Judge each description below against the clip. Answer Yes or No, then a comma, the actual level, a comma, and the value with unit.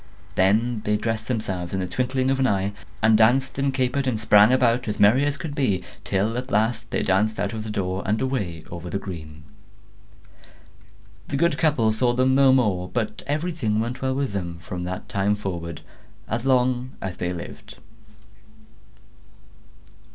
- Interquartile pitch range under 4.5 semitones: No, average, 4.9 semitones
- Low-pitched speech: Yes, low, 110 Hz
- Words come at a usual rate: Yes, average, 175 wpm